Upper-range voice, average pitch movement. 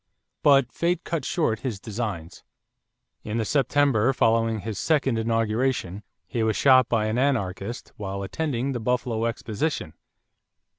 No: low, 115 Hz; average, 3.7 semitones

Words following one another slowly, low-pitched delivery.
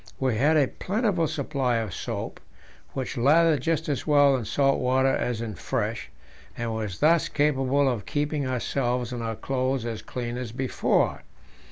No: average, 165 wpm; low, 130 Hz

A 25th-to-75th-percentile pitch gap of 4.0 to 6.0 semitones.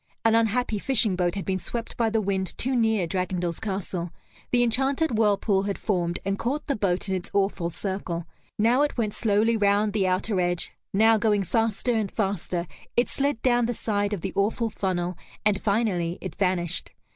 No: average, 3.4 semitones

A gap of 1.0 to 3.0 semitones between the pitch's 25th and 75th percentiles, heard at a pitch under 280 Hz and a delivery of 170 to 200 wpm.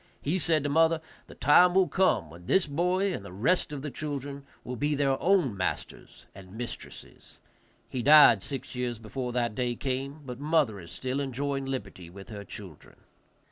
No: average, 4.8 semitones; low, 135 Hz; average, 180 wpm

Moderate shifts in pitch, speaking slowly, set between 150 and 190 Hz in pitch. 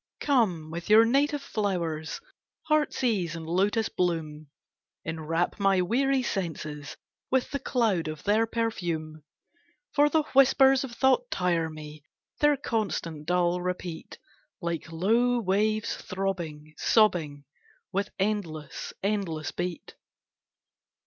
No: wide, 6.1 semitones; slow, 110 wpm; medium, 185 Hz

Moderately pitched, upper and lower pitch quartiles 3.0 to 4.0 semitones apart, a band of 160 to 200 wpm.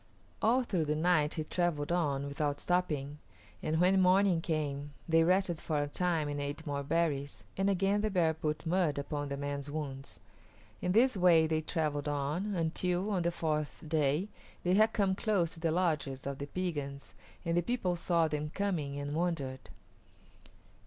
Yes: medium, 160 Hz; average, 3.7 semitones; average, 175 wpm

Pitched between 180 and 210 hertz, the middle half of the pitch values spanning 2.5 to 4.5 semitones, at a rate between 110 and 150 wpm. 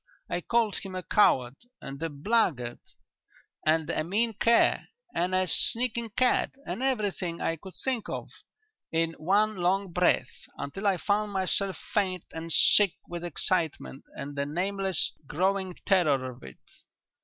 Yes: medium, 185 Hz; average, 4.1 semitones; average, 145 wpm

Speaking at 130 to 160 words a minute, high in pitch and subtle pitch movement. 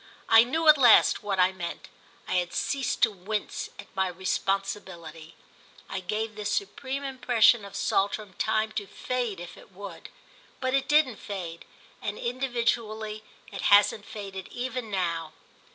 No: average, 145 wpm; high, 210 Hz; average, 4.2 semitones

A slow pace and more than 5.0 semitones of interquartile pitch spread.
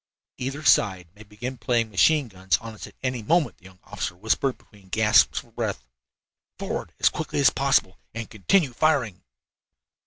No: average, 165 wpm; wide, 5.4 semitones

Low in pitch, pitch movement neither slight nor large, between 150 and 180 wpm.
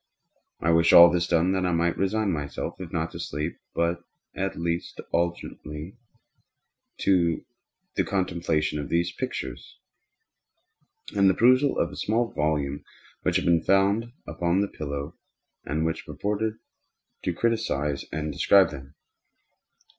No: very low, 85 Hz; average, 4.1 semitones; slow, 135 wpm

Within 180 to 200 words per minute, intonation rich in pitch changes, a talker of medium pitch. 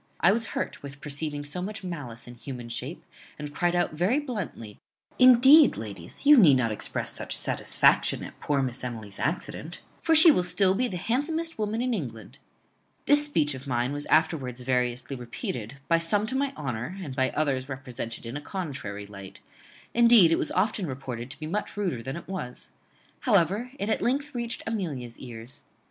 Yes: average, 185 wpm; wide, 8.9 semitones; medium, 150 Hz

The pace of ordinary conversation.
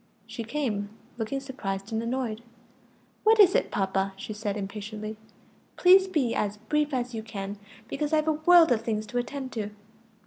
Yes: average, 170 wpm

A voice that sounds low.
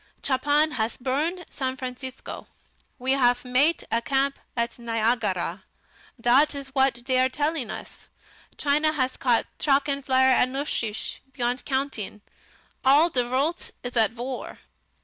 No: very high, 260 Hz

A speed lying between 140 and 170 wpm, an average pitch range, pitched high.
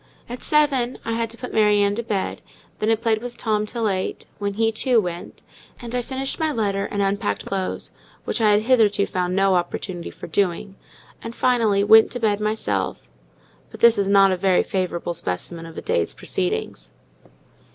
No: average, 190 wpm; average, 3.5 semitones; high, 205 Hz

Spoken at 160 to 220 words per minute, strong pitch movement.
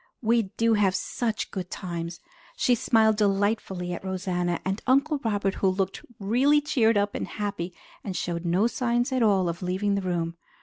No: average, 180 wpm; average, 3.8 semitones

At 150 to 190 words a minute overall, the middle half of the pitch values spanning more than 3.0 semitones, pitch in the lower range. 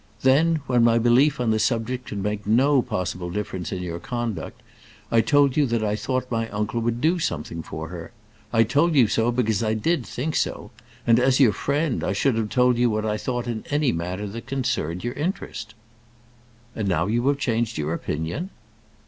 No: average, 200 wpm; average, 3.8 semitones; low, 115 Hz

